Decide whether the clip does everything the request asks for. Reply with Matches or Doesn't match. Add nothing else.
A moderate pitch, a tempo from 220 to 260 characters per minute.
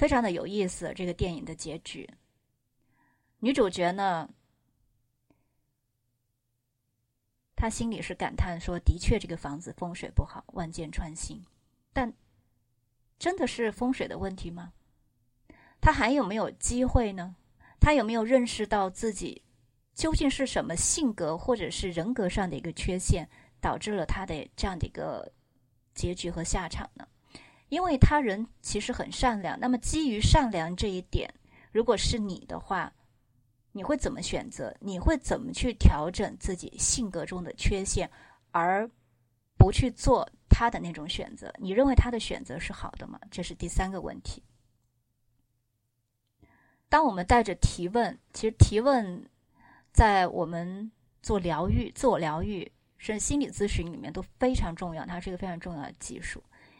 Matches